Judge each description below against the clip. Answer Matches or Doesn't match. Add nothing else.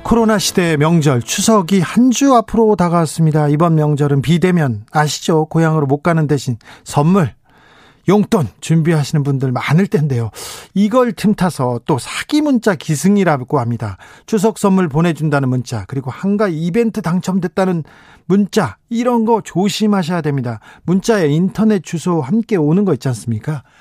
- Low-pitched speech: Doesn't match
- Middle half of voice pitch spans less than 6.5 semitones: Matches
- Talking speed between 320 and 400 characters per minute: Matches